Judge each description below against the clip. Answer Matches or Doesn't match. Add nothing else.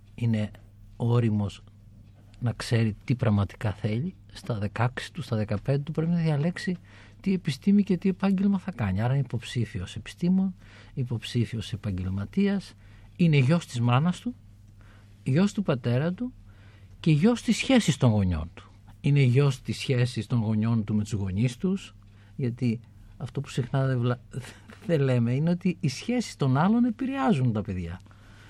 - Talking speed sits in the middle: Matches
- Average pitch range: Doesn't match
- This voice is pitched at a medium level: Doesn't match